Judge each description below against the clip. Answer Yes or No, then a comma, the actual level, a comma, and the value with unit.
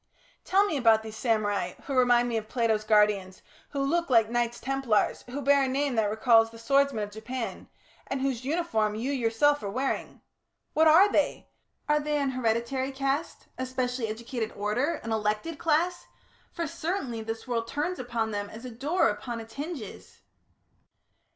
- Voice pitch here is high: Yes, high, 245 Hz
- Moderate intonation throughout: Yes, average, 4.1 semitones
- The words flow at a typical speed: Yes, average, 170 wpm